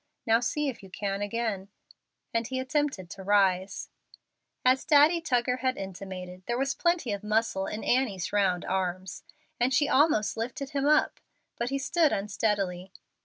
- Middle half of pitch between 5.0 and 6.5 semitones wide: Yes, wide, 5.6 semitones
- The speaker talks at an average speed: Yes, average, 160 wpm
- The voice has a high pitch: Yes, high, 225 Hz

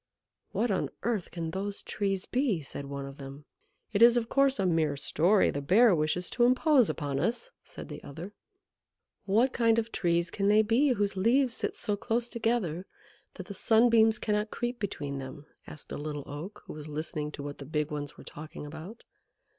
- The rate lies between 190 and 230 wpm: Yes, average, 195 wpm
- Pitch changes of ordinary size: No, wide, 7.1 semitones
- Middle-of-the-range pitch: No, high, 195 Hz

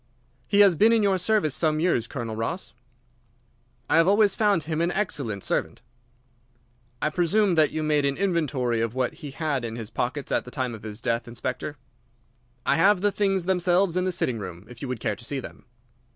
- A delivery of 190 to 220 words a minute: Yes, fast, 205 wpm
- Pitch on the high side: No, medium, 155 Hz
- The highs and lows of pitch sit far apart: Yes, wide, 7.2 semitones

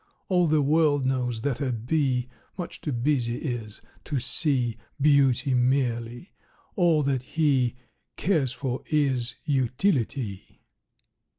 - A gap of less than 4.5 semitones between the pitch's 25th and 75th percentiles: Yes, average, 3.5 semitones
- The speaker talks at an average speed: No, slow, 115 wpm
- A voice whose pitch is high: No, low, 135 Hz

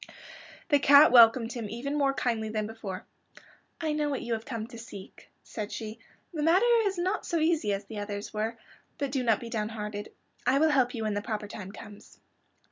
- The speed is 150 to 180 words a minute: No, fast, 205 wpm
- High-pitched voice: Yes, high, 230 Hz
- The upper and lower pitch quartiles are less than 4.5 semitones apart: No, average, 4.8 semitones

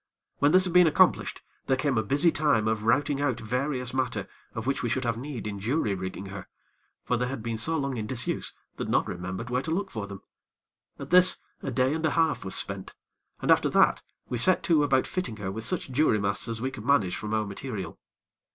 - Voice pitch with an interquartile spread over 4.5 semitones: Yes, average, 5.2 semitones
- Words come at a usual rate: No, fast, 225 wpm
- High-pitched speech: No, low, 125 Hz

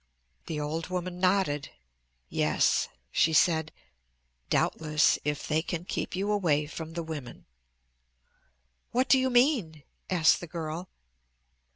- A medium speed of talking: No, slow, 125 wpm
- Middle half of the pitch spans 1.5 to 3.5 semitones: Yes, average, 3.1 semitones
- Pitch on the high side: No, medium, 165 Hz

